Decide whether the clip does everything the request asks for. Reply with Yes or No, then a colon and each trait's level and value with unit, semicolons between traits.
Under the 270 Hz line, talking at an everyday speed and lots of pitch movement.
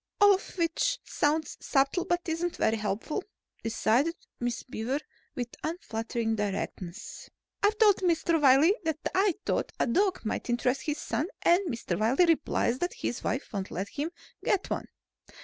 No: very high, 290 Hz; average, 155 wpm; wide, 7.2 semitones